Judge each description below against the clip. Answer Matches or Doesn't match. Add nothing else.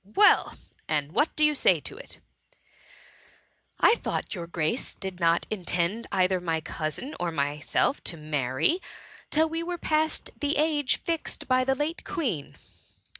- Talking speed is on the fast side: Doesn't match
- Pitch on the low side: Doesn't match